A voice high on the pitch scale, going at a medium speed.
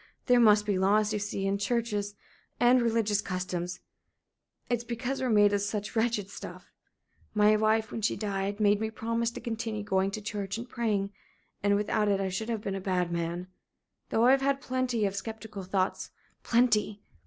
Yes: high, 210 Hz; average, 180 wpm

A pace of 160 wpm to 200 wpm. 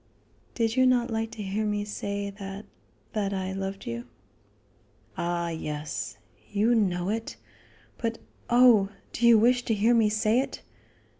No: average, 150 wpm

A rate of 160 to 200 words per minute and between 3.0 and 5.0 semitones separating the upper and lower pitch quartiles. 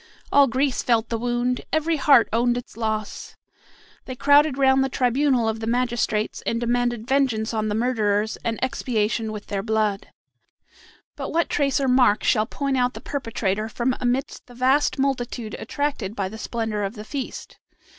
Yes: average, 170 wpm; average, 3.3 semitones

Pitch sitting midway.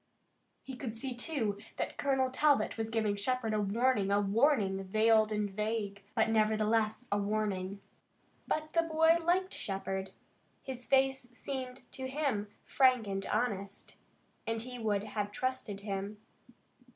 No: high, 220 Hz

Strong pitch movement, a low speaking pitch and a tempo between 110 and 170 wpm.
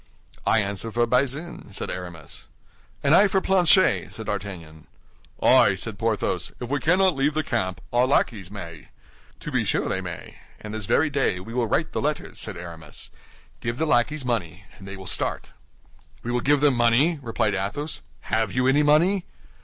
No: wide, 7.1 semitones; low, 120 Hz; average, 180 wpm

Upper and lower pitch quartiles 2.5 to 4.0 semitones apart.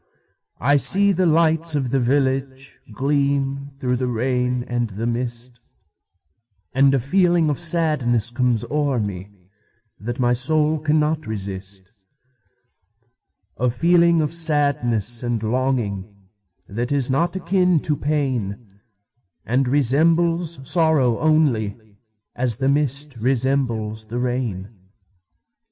No: average, 4.7 semitones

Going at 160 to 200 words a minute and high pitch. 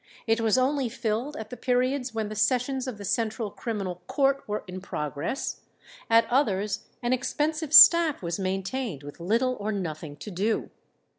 Yes: average, 165 wpm; high, 225 Hz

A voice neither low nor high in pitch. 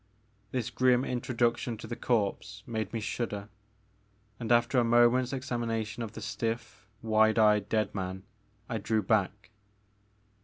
No: low, 115 Hz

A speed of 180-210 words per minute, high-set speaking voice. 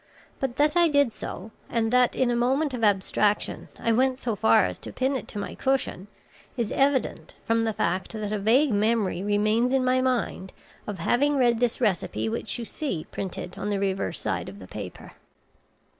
Yes: average, 200 wpm; high, 230 Hz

